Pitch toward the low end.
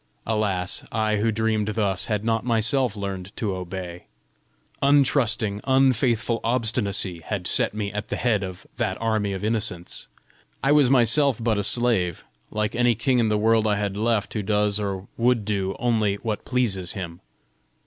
Yes: low, 110 Hz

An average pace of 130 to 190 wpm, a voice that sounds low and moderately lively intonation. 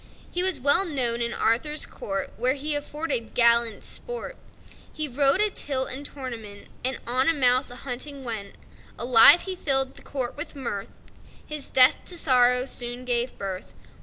No: average, 165 wpm; very high, 260 Hz; average, 3.4 semitones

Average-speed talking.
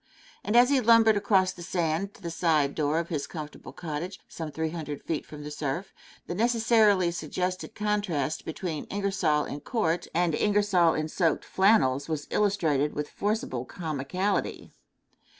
Yes: average, 155 wpm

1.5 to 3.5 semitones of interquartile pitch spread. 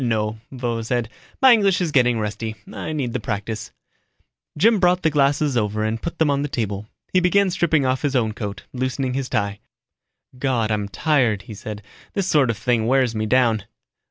No: average, 5.2 semitones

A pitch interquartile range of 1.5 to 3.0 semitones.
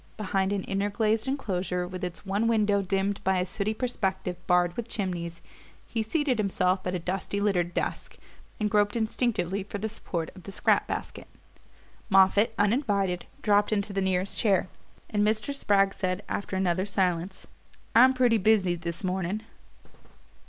Yes: narrow, 2.6 semitones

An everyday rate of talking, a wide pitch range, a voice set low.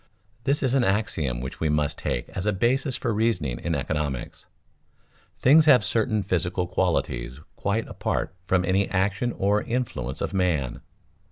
Yes: average, 160 wpm; wide, 7.2 semitones; very low, 95 Hz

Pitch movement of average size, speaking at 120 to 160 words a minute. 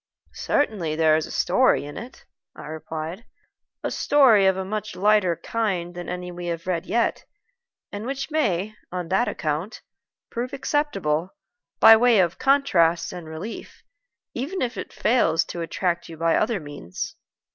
No: wide, 5.7 semitones; average, 155 wpm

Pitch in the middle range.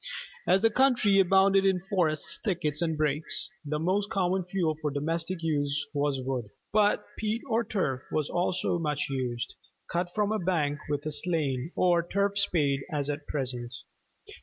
Yes: medium, 165 Hz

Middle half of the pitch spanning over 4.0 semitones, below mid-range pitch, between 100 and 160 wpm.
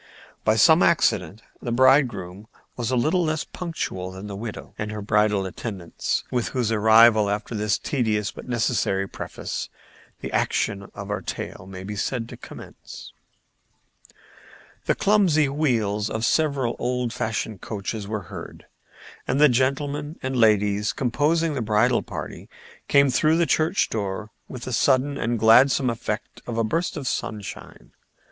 Yes: average, 4.6 semitones; low, 115 Hz; average, 150 wpm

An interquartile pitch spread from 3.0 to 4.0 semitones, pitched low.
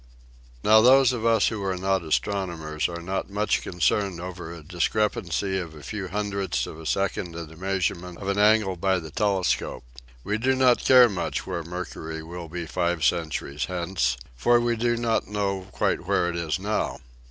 Yes: average, 3.6 semitones; very low, 95 Hz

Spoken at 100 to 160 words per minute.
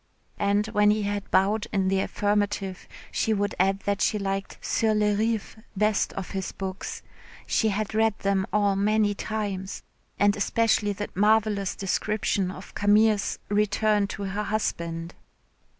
Yes: average, 150 wpm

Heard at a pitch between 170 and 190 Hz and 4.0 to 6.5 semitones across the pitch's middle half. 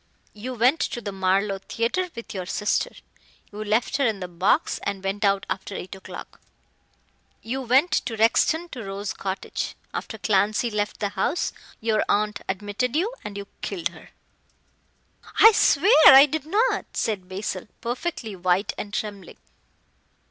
No: high, 210 Hz; average, 4.4 semitones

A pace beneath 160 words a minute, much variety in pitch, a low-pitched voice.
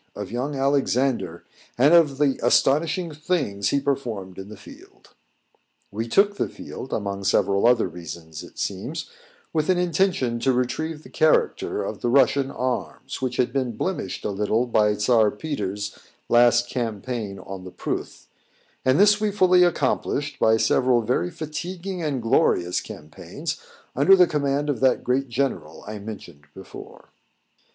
Yes: average, 150 wpm; wide, 6.1 semitones; low, 125 Hz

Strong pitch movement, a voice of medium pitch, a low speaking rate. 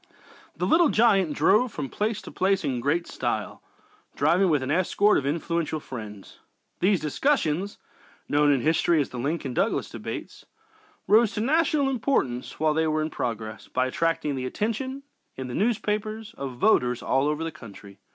No: wide, 7.7 semitones; medium, 160 Hz; average, 165 wpm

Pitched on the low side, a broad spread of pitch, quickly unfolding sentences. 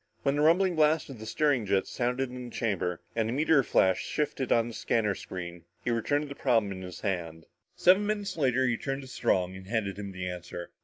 Yes: low, 115 Hz; wide, 6.8 semitones; fast, 225 wpm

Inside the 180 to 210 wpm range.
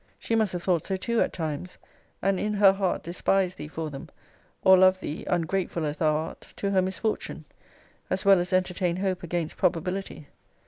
Yes: average, 185 wpm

